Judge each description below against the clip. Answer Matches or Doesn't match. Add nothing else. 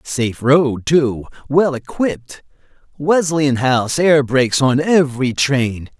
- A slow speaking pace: Matches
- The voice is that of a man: Matches